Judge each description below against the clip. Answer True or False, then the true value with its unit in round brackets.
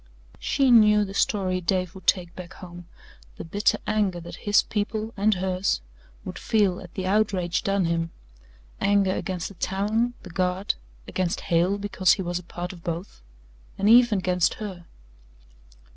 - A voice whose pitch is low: False (190 Hz)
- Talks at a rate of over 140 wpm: True (160 wpm)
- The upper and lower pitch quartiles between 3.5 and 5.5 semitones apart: False (2.6 semitones)